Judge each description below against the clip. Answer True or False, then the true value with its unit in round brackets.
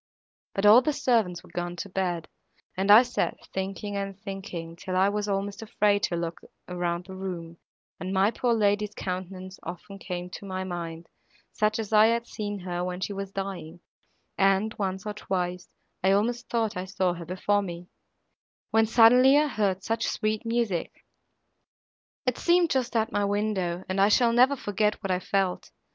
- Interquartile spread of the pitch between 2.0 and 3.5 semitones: True (2.9 semitones)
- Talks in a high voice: True (195 Hz)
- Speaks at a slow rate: False (175 wpm)